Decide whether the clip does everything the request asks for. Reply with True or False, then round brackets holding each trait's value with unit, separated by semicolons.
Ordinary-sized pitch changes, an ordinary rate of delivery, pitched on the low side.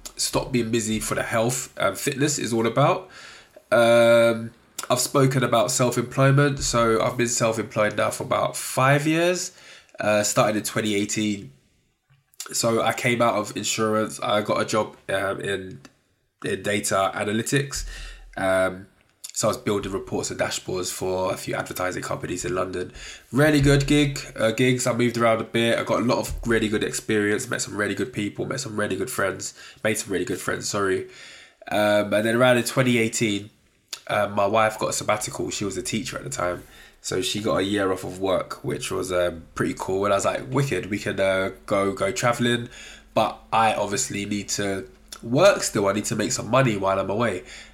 True (3.5 semitones; 190 wpm; 110 Hz)